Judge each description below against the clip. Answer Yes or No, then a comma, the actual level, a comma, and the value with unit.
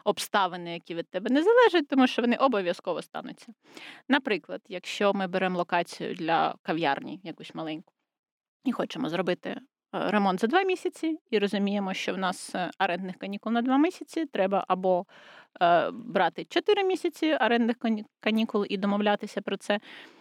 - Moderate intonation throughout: No, wide, 7.8 semitones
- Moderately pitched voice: No, high, 220 Hz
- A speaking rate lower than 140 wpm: No, average, 145 wpm